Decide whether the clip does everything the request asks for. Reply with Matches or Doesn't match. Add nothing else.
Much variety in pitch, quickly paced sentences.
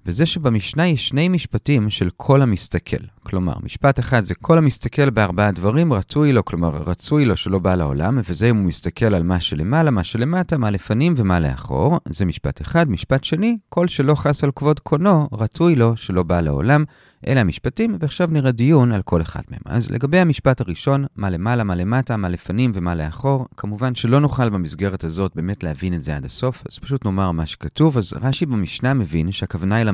Matches